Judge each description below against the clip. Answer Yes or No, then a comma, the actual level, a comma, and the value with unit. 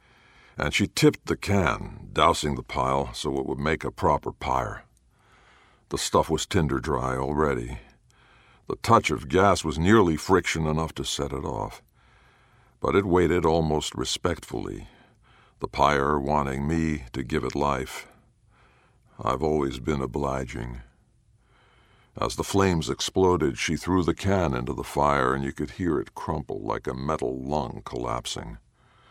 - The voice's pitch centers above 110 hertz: No, very low, 75 Hz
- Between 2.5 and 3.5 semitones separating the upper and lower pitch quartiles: No, average, 4.3 semitones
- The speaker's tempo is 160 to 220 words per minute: No, average, 150 wpm